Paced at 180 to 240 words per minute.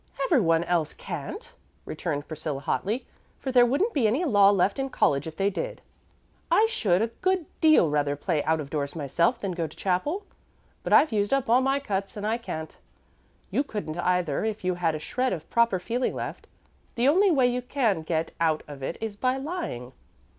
Yes: average, 200 wpm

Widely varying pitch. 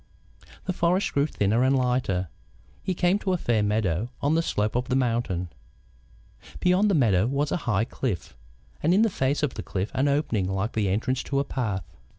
Yes: wide, 6.2 semitones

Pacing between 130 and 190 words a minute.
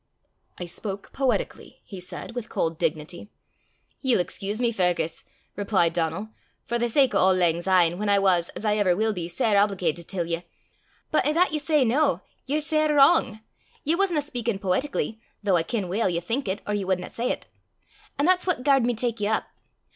No: average, 200 wpm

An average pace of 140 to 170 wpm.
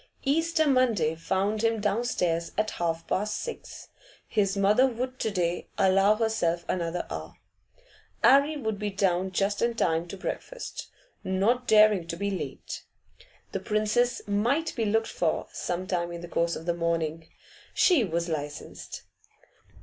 Yes: average, 150 wpm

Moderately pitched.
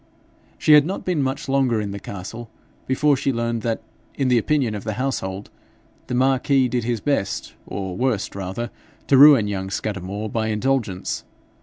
No: low, 120 Hz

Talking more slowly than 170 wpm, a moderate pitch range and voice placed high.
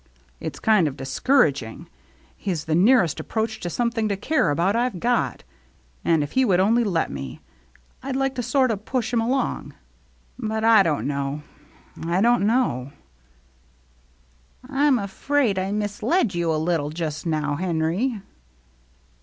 No: average, 160 wpm; wide, 7.3 semitones; high, 195 Hz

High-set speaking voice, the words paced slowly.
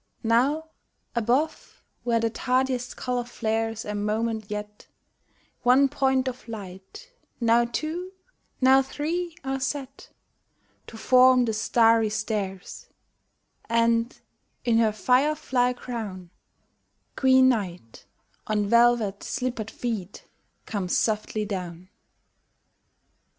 Yes: high, 235 Hz; slow, 105 wpm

